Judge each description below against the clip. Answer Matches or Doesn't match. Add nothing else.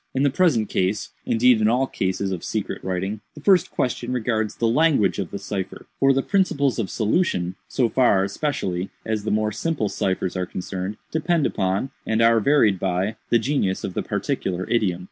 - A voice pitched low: Matches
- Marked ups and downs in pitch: Matches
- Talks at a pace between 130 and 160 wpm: Doesn't match